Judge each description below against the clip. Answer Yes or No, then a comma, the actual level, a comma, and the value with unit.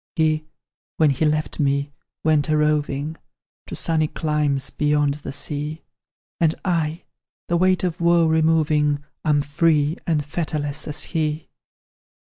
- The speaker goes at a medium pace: No, slow, 130 wpm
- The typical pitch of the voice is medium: Yes, medium, 155 Hz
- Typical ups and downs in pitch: No, narrow, 1.6 semitones